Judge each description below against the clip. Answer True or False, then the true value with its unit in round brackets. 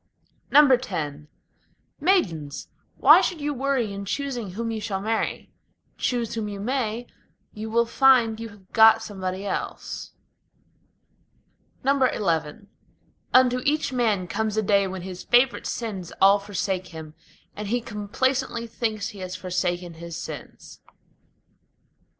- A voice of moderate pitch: False (215 Hz)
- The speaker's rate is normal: False (125 wpm)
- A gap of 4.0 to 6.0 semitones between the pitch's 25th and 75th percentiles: True (4.5 semitones)